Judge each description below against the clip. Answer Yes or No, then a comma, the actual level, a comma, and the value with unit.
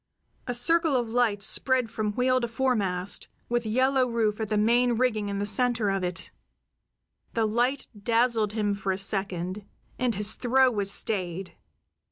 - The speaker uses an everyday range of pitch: Yes, average, 3.5 semitones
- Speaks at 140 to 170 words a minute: Yes, average, 165 wpm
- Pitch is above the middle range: Yes, high, 225 Hz